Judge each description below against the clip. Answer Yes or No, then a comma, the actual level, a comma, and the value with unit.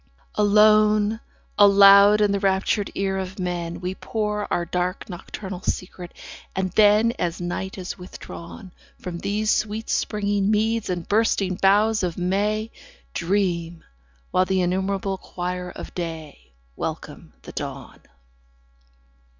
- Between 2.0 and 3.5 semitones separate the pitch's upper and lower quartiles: Yes, narrow, 2.6 semitones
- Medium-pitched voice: No, high, 195 Hz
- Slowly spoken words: Yes, slow, 125 wpm